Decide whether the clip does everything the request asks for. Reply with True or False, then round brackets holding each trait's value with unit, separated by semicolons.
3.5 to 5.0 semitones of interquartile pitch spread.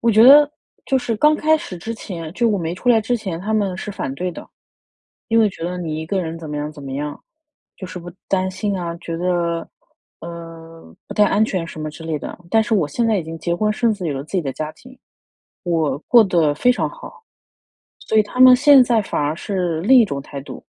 False (5.4 semitones)